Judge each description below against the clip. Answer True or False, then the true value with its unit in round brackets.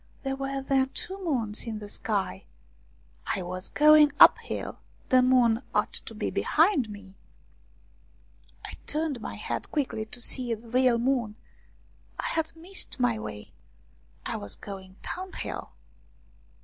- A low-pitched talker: False (250 Hz)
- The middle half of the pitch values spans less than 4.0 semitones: False (5.2 semitones)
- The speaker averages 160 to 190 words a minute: False (135 wpm)